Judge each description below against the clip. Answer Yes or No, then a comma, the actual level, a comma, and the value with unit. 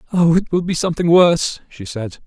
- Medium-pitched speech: Yes, medium, 160 Hz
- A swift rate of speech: Yes, fast, 210 wpm